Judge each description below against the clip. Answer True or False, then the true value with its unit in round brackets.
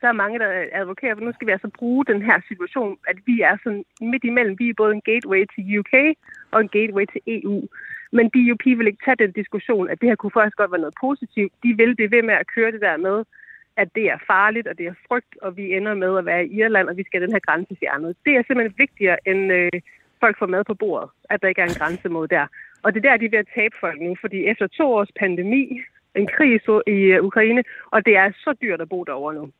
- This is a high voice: True (215 Hz)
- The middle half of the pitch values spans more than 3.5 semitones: True (3.9 semitones)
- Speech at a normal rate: False (260 wpm)